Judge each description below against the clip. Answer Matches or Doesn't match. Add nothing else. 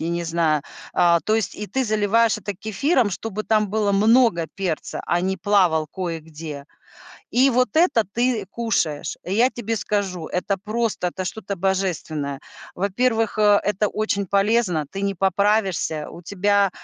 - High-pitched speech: Matches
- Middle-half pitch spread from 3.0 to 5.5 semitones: Matches